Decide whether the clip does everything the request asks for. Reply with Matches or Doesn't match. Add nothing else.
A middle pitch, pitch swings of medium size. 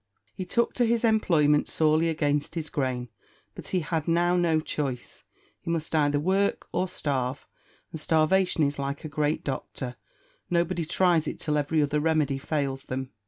Matches